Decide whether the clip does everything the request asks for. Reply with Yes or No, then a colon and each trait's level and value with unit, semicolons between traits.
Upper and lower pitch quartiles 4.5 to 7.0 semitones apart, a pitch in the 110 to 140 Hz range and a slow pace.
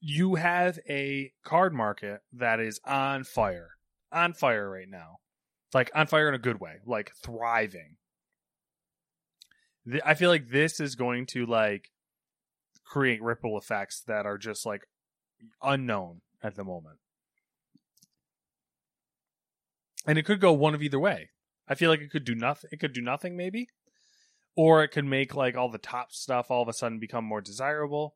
No: average, 4.8 semitones; low, 135 Hz; average, 165 wpm